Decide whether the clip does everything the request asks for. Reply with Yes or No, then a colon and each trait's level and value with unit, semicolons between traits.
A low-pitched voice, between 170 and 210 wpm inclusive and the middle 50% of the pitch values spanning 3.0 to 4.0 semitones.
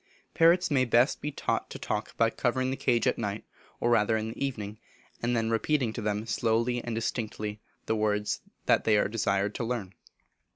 No: low, 115 Hz; average, 190 wpm; narrow, 2.5 semitones